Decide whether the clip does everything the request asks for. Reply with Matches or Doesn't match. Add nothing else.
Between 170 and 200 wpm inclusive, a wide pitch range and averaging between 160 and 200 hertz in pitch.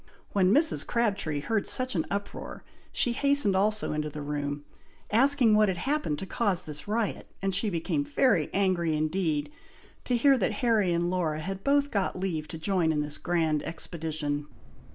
Matches